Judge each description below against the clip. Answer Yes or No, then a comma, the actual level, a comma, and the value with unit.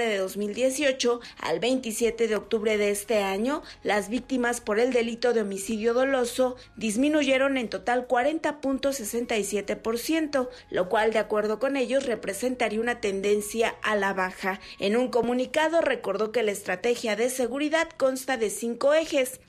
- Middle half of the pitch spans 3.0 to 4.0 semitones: Yes, average, 3.4 semitones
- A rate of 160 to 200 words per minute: No, average, 140 wpm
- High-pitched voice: Yes, high, 240 Hz